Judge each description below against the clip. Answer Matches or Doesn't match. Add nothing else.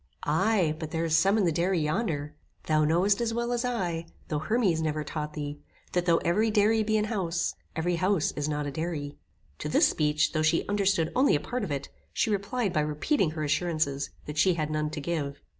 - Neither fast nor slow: Doesn't match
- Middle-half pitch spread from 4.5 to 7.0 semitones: Matches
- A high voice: Doesn't match